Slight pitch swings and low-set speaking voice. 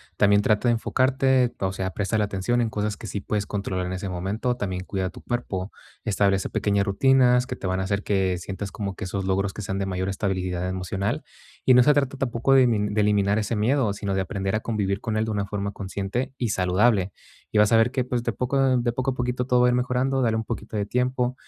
No: average, 4.1 semitones; low, 105 Hz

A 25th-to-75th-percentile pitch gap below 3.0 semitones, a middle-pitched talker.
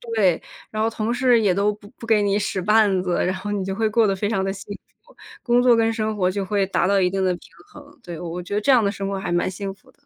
No: narrow, 2.6 semitones; high, 205 Hz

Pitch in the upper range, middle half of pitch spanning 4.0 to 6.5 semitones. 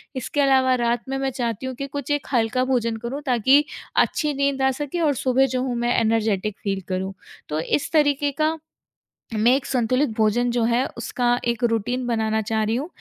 No: high, 245 Hz; average, 3.1 semitones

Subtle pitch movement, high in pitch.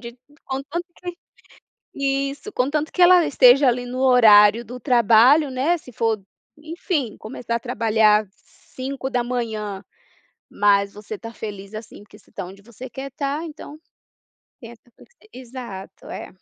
No: average, 4.3 semitones; high, 245 Hz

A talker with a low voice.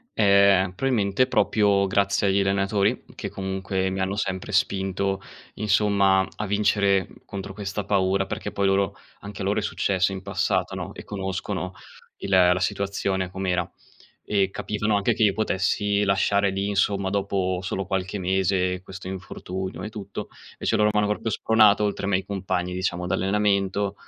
Yes: low, 100 Hz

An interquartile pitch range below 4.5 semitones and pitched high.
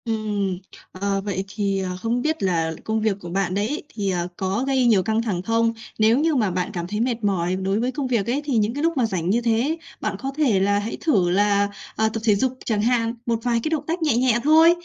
Yes: average, 4.1 semitones; high, 220 Hz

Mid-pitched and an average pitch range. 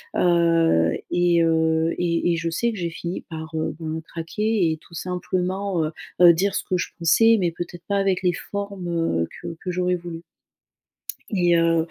No: medium, 170 Hz; narrow, 1.8 semitones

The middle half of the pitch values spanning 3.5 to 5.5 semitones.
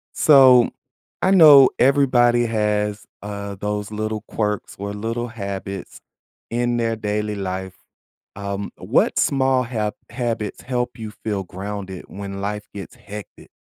No: average, 3.1 semitones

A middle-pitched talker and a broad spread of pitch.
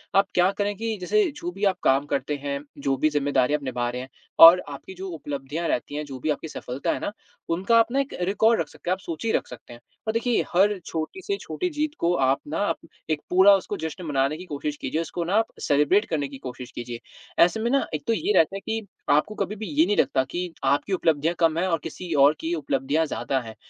Yes: medium, 165 Hz; wide, 6.0 semitones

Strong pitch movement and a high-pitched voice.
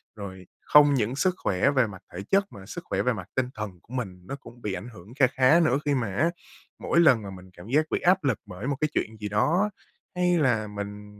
No: wide, 6.0 semitones; low, 120 Hz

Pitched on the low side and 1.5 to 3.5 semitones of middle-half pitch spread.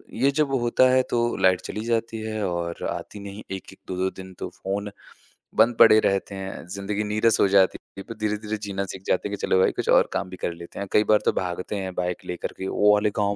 Yes: low, 100 Hz; narrow, 2.4 semitones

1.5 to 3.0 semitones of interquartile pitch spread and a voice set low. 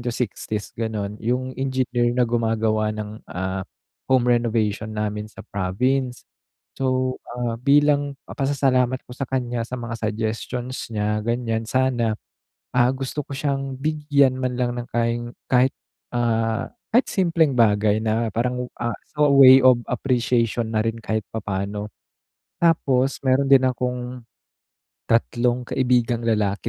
Yes: average, 2.7 semitones; low, 120 Hz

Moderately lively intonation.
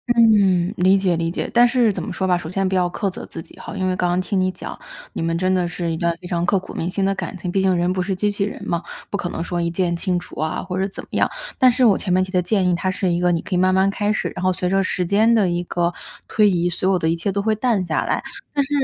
No: narrow, 2.2 semitones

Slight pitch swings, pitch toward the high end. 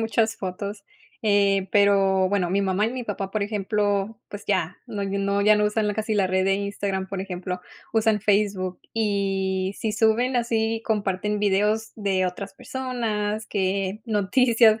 Yes: narrow, 2.1 semitones; high, 205 Hz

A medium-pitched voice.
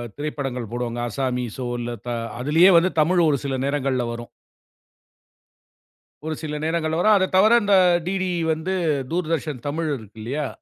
Yes: medium, 150 Hz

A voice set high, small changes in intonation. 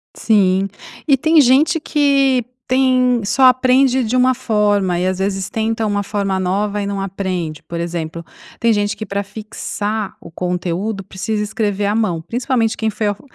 No: high, 210 Hz; average, 4.2 semitones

